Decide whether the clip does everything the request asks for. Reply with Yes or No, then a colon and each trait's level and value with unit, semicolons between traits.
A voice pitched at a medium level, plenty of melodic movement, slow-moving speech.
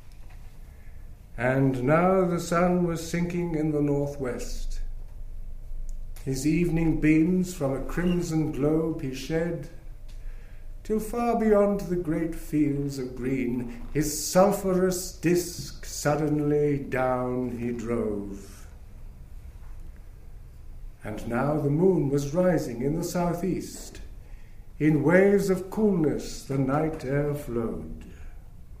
Yes: medium, 145 Hz; wide, 7.4 semitones; slow, 105 wpm